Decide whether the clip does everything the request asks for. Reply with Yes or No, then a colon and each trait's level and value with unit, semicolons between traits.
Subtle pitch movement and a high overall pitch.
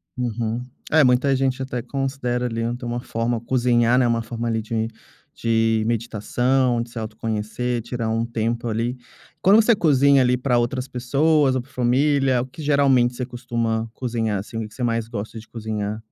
No: narrow, 2.2 semitones; low, 120 Hz